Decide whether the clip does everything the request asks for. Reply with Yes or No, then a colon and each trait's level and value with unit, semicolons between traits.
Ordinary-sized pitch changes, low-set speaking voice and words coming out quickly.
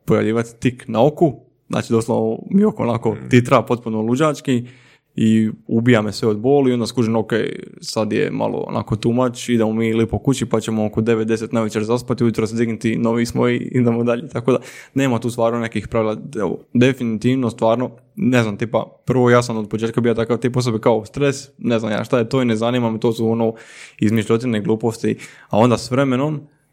No: narrow, 2.0 semitones; low, 115 Hz; fast, 195 wpm